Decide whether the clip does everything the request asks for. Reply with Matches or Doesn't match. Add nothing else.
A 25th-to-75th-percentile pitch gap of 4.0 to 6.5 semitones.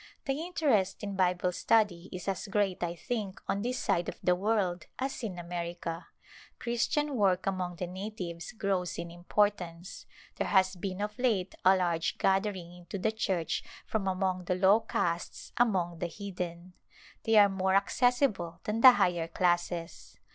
Doesn't match